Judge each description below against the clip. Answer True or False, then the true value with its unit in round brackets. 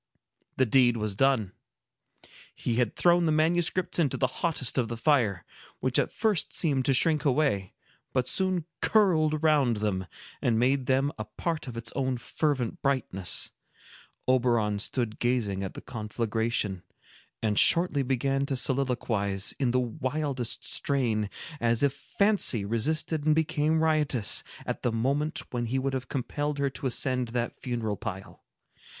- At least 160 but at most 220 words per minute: False (150 wpm)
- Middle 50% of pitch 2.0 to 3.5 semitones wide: False (4.4 semitones)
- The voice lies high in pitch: False (130 Hz)